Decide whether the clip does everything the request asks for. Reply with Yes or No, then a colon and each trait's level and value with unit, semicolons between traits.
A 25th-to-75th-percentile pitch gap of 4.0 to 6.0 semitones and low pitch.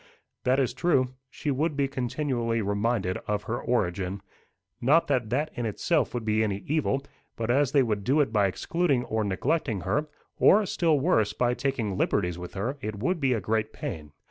Yes: average, 5.1 semitones; low, 120 Hz